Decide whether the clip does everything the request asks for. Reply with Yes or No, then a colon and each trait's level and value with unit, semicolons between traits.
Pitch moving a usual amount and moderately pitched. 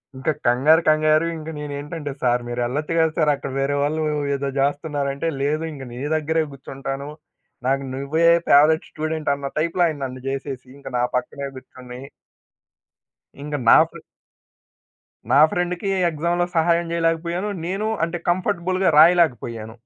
Yes: average, 3.2 semitones; medium, 150 Hz